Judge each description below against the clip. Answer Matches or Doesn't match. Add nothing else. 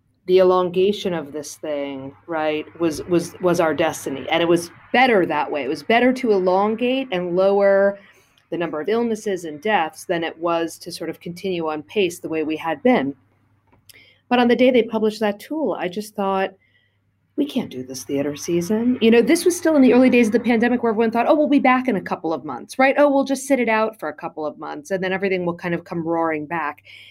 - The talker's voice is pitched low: Doesn't match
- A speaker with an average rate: Doesn't match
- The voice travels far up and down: Matches